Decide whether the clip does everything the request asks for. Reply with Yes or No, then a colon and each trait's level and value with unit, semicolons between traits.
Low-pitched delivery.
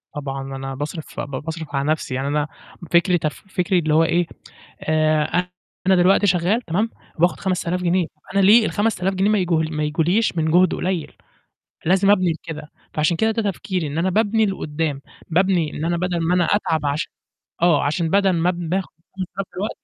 No: medium, 175 Hz